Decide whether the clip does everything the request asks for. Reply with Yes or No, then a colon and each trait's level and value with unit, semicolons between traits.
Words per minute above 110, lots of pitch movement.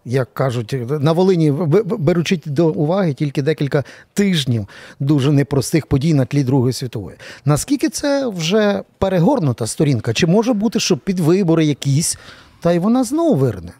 Yes: average, 150 wpm; wide, 5.9 semitones